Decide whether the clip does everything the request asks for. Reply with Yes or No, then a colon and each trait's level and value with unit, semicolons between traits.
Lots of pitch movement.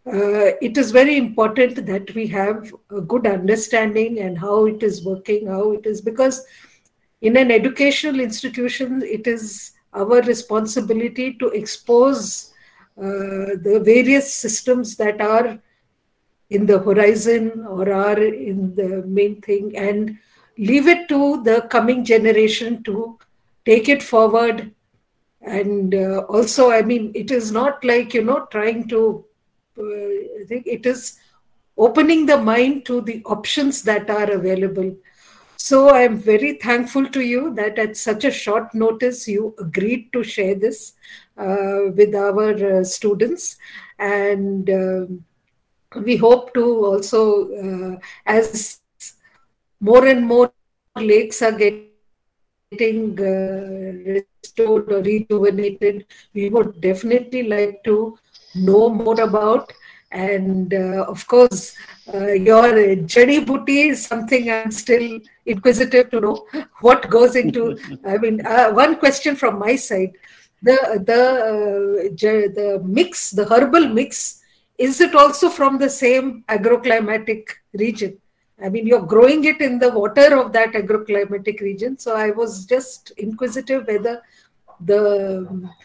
No: average, 3.4 semitones